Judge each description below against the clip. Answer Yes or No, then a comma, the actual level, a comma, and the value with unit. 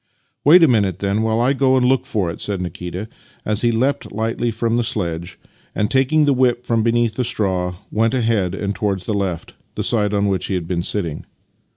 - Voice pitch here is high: No, low, 110 Hz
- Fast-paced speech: Yes, fast, 225 wpm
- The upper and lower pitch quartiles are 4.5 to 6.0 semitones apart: No, average, 3.9 semitones